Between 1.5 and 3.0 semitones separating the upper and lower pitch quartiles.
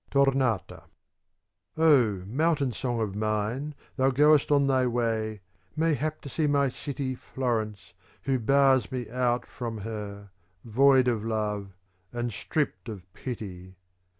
No: average, 4.3 semitones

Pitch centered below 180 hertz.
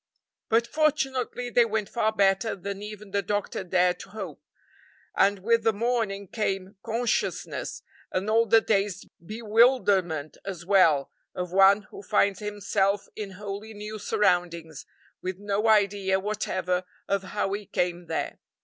No: high, 200 Hz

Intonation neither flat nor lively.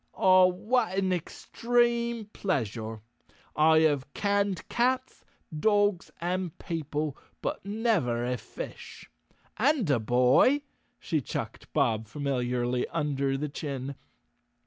No: wide, 7.5 semitones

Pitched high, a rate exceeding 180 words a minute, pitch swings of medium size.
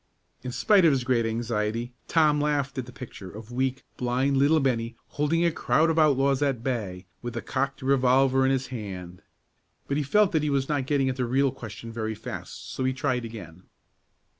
No: low, 130 Hz; average, 200 wpm; average, 3.1 semitones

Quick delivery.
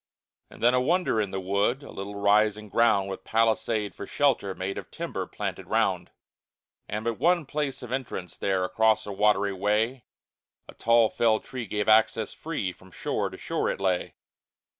No: average, 180 wpm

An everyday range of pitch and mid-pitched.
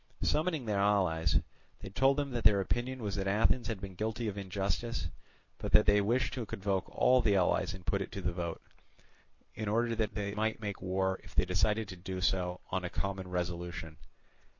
No: average, 3.2 semitones; low, 100 Hz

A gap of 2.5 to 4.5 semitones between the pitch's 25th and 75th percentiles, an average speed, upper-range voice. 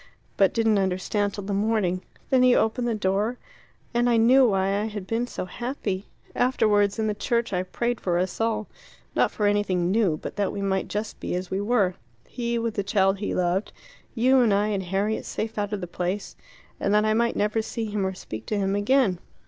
No: average, 2.8 semitones; fast, 215 wpm; high, 205 Hz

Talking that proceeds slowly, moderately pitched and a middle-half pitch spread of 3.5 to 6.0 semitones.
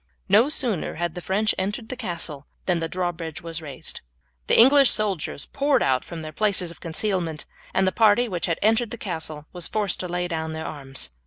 No: average, 200 wpm; medium, 180 Hz; average, 4.9 semitones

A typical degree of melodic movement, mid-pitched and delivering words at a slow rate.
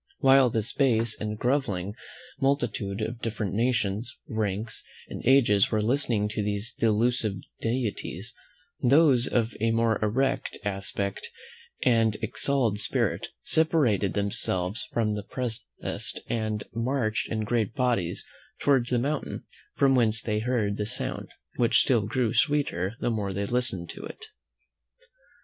No: average, 3.2 semitones; low, 115 Hz; slow, 130 wpm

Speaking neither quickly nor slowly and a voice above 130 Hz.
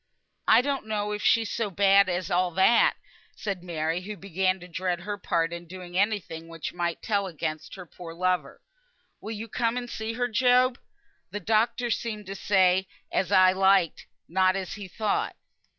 Yes: average, 180 wpm; high, 190 Hz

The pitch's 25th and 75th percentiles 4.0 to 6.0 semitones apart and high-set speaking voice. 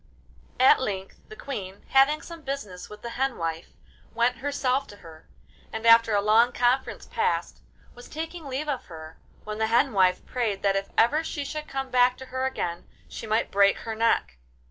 Yes: average, 5.0 semitones; high, 235 Hz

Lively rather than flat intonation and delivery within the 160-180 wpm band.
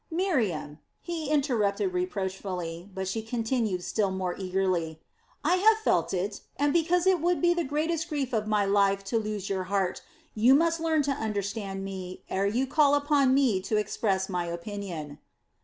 Yes: wide, 7.4 semitones; average, 170 wpm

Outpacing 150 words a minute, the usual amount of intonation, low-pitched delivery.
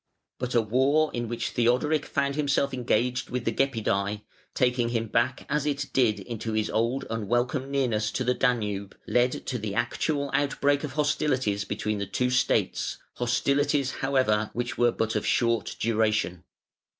Yes: average, 160 wpm; average, 3.8 semitones; low, 120 Hz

